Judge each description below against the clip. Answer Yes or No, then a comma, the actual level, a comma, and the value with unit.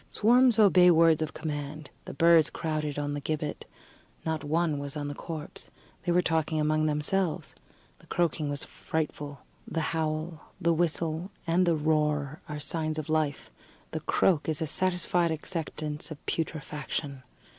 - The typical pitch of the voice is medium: Yes, medium, 155 Hz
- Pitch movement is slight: Yes, narrow, 2.0 semitones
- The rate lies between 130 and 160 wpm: Yes, average, 155 wpm